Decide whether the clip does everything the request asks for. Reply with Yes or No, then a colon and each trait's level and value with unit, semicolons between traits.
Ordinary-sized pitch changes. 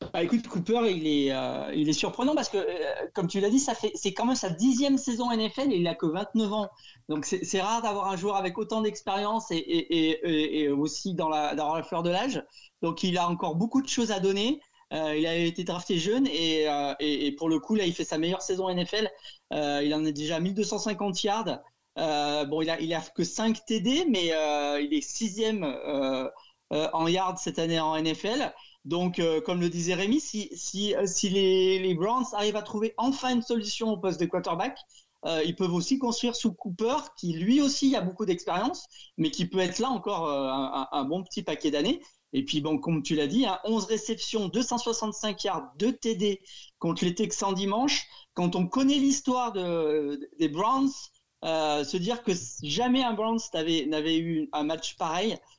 No: wide, 5.9 semitones